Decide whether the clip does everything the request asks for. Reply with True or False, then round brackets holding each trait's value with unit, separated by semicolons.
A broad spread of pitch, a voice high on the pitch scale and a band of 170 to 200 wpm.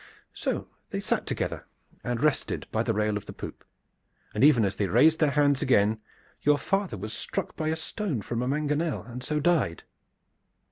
False (5.8 semitones; 135 Hz; 185 wpm)